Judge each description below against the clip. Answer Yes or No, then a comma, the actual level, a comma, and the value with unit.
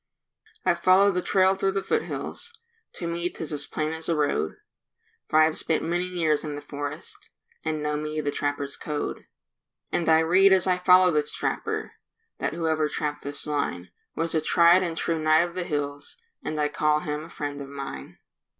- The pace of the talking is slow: No, average, 190 wpm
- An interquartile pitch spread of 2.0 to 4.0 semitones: Yes, average, 2.8 semitones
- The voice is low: No, medium, 155 Hz